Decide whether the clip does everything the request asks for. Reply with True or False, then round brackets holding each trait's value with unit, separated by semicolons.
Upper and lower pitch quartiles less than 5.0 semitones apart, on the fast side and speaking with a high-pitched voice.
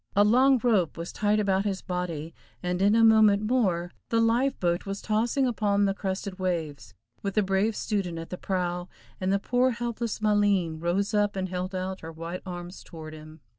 False (3.3 semitones; 195 wpm; 195 Hz)